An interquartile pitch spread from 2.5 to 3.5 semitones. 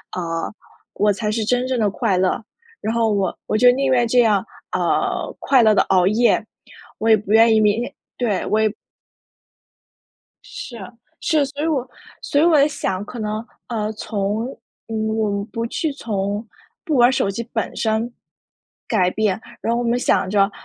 Yes: average, 2.8 semitones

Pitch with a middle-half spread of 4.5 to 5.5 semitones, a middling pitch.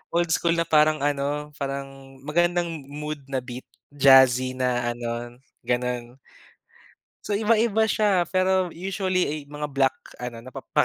Yes: average, 5.1 semitones; medium, 145 Hz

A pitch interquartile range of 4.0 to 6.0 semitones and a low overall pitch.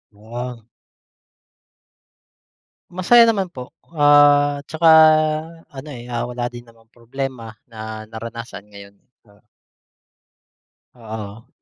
Yes: average, 4.3 semitones; low, 120 Hz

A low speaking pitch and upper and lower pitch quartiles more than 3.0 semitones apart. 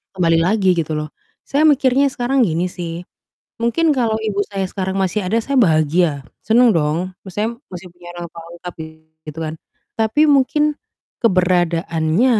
No: medium, 185 Hz; wide, 5.6 semitones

